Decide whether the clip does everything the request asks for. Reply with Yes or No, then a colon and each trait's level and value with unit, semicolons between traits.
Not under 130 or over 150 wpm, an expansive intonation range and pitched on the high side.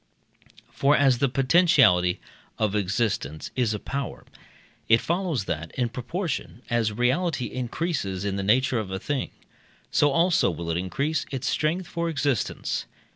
No: average, 145 wpm; wide, 6.3 semitones; low, 125 Hz